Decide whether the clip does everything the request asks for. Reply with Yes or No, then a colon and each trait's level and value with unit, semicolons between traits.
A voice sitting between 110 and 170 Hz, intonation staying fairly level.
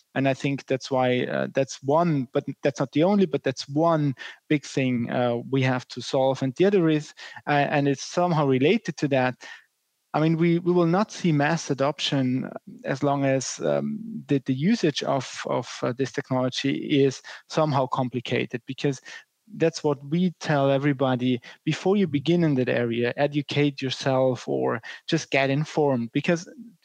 No: medium, 140 Hz; average, 3.1 semitones